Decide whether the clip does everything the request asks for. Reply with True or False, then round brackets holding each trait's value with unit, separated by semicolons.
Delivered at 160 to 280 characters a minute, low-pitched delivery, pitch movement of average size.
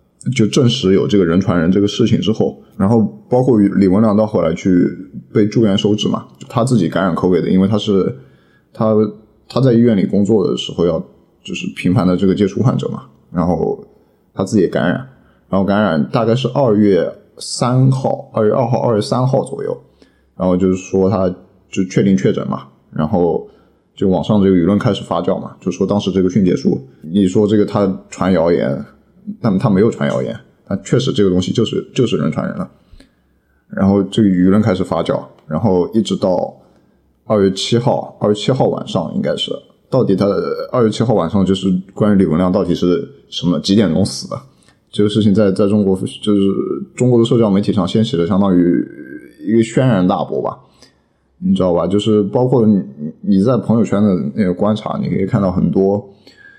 False (290 characters per minute; 105 Hz; 3.2 semitones)